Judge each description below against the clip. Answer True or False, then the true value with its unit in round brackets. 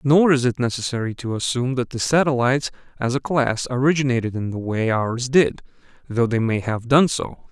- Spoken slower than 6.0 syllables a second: True (5.5 syllables/s)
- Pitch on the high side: False (125 Hz)